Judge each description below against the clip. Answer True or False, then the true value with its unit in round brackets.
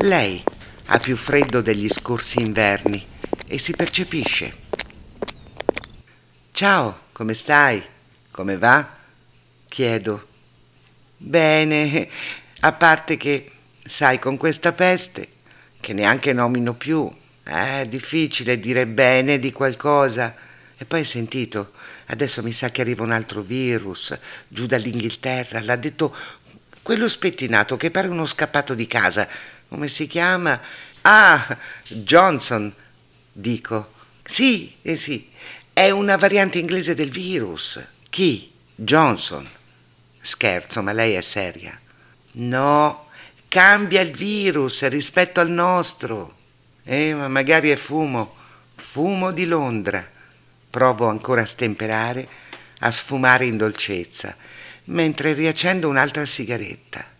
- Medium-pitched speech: False (130 Hz)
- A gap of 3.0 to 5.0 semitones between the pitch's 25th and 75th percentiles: False (5.6 semitones)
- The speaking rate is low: True (110 wpm)